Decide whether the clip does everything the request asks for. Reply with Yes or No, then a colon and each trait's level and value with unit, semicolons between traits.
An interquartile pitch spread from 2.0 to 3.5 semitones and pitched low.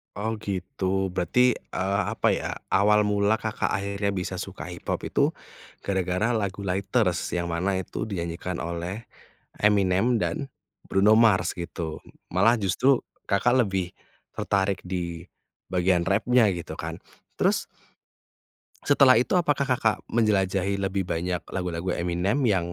Yes: average, 3.1 semitones; very low, 95 Hz